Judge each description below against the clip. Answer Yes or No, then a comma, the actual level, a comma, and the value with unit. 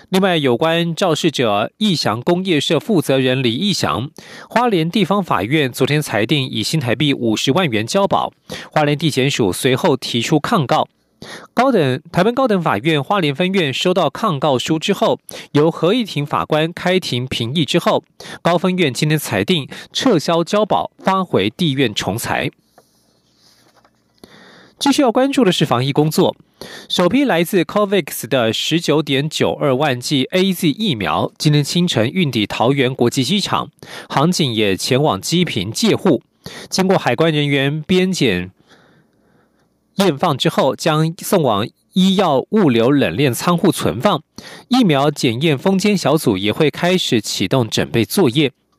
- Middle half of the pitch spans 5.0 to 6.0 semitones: Yes, wide, 5.6 semitones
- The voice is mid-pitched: Yes, medium, 160 Hz